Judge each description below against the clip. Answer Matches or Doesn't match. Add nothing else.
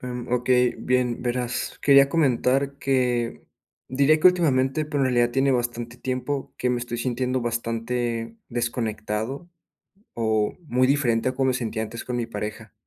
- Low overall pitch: Matches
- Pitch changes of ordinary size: Doesn't match